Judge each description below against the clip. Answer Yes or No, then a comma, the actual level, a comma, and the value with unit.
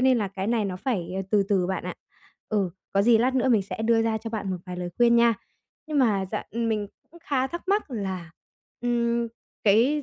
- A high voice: Yes, high, 225 Hz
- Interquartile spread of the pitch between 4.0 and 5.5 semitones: No, average, 3.5 semitones